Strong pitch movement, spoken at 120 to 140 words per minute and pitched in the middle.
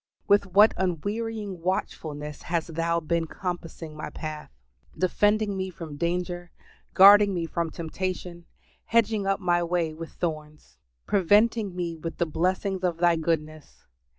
No: average, 2.9 semitones; slow, 135 wpm; medium, 175 Hz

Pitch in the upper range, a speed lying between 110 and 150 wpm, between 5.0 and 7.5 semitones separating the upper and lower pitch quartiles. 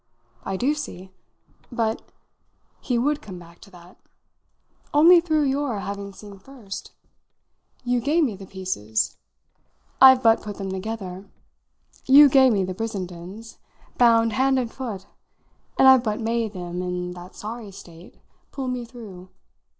Yes: high, 220 Hz; average, 140 wpm; average, 5.3 semitones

